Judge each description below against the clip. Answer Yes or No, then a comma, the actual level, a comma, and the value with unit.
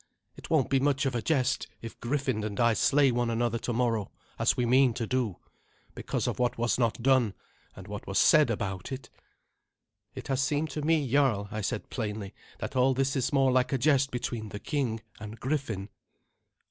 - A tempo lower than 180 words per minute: No, average, 195 wpm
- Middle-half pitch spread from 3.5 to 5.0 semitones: No, average, 3.1 semitones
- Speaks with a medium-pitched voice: No, low, 125 Hz